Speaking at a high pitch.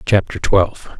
No: very low, 95 Hz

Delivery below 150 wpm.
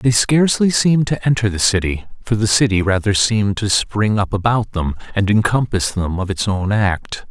No: average, 195 wpm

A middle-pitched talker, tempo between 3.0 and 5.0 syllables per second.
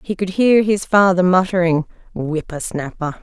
Yes: medium, 180 Hz; 4.6 syllables/s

